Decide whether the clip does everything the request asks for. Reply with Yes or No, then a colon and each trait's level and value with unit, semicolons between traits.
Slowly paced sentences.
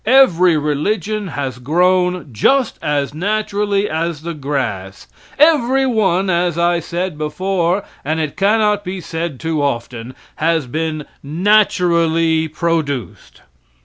Yes: slow, 115 wpm